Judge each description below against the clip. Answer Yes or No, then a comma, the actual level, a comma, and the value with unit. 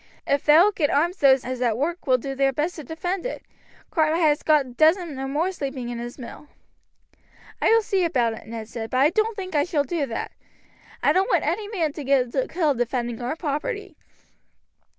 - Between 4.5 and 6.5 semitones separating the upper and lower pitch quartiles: Yes, average, 5.2 semitones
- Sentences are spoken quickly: Yes, fast, 220 wpm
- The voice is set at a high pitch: Yes, very high, 295 Hz